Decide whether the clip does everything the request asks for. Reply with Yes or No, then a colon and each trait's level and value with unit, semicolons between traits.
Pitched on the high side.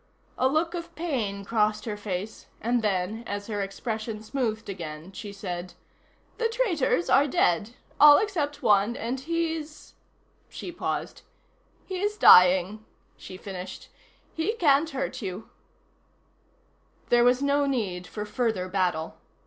Yes: high, 220 Hz